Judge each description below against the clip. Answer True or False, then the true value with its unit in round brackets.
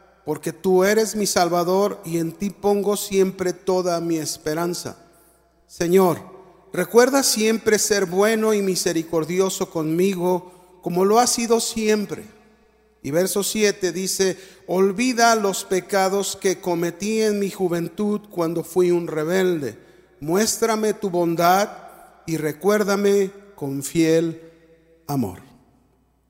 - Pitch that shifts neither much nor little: True (3.2 semitones)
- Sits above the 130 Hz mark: True (185 Hz)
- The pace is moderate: False (115 wpm)